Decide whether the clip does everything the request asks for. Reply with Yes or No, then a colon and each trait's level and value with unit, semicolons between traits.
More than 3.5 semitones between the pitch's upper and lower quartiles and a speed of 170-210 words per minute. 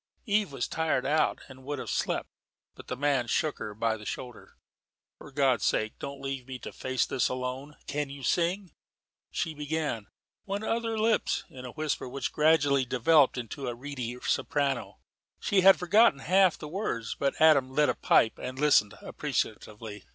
Yes: average, 3.9 semitones; average, 175 wpm